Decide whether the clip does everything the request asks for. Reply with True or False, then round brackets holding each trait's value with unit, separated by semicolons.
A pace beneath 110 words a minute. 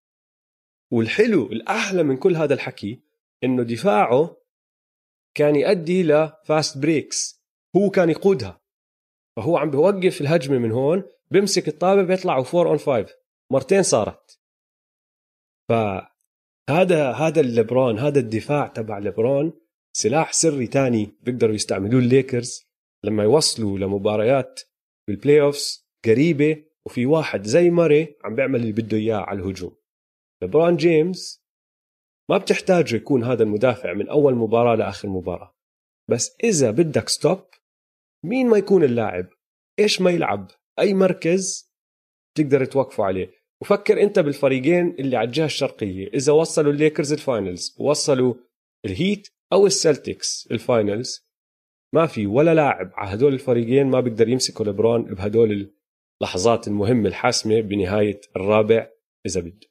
False (125 wpm)